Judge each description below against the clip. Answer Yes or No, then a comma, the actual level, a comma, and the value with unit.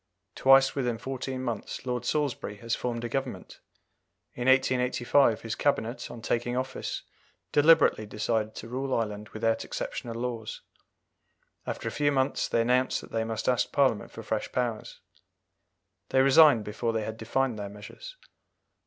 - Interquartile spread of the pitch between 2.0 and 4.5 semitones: Yes, average, 2.9 semitones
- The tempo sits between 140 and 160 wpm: Yes, average, 150 wpm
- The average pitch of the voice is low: Yes, low, 120 Hz